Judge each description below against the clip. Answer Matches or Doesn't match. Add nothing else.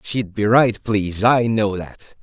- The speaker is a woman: Doesn't match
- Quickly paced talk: Doesn't match